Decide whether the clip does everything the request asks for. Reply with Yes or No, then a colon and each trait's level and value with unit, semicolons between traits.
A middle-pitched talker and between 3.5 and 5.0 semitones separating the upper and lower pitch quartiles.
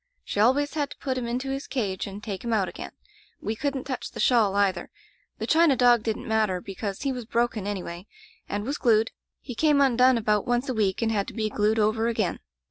No: high, 225 Hz; average, 3.8 semitones